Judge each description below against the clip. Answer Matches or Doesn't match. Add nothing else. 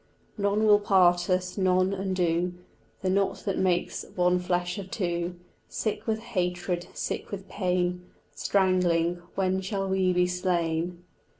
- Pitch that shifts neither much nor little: Doesn't match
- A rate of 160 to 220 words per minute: Doesn't match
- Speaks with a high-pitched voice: Doesn't match